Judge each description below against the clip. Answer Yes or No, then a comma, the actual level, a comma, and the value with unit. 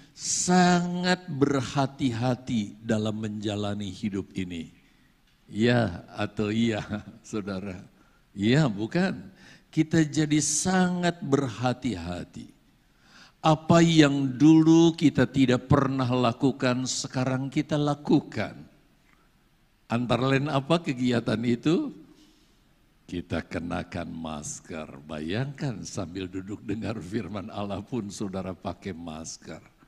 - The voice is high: No, low, 120 Hz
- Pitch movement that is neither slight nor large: No, wide, 6.2 semitones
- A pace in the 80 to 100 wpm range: Yes, average, 90 wpm